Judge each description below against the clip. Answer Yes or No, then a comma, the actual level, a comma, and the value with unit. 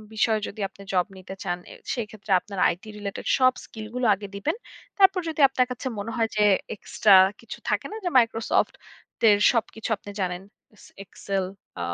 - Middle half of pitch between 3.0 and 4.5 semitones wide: Yes, average, 3.8 semitones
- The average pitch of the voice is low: No, high, 215 Hz